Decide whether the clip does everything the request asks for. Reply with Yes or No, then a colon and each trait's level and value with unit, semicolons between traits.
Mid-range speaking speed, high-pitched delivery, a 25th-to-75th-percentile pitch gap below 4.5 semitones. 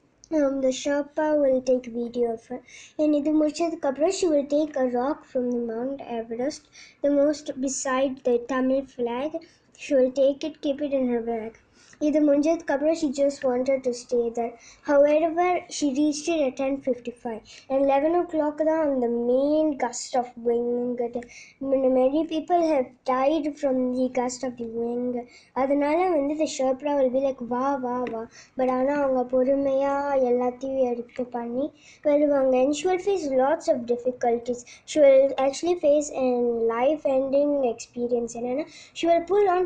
No: fast, 150 wpm; very high, 270 Hz; average, 3.2 semitones